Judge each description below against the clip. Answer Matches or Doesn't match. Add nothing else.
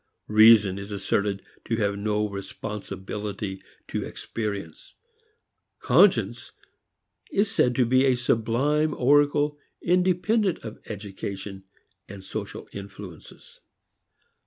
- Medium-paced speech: Doesn't match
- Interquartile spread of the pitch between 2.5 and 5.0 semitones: Doesn't match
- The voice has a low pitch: Matches